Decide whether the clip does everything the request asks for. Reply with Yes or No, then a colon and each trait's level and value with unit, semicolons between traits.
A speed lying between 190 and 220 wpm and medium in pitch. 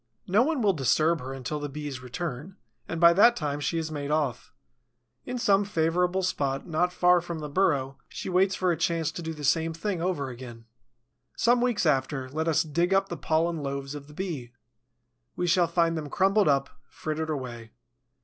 Yes: average, 195 wpm; medium, 160 Hz